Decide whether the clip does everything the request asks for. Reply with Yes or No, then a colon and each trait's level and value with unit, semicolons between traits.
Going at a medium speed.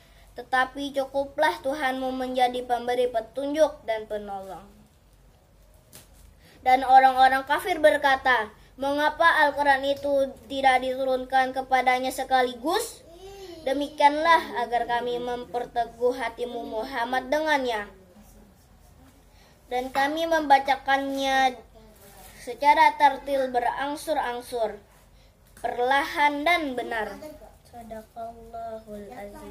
No: slow, 75 wpm